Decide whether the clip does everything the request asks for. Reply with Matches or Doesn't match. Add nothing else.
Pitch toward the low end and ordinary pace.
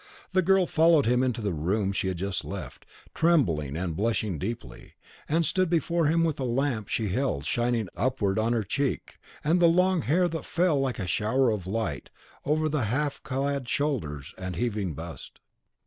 Matches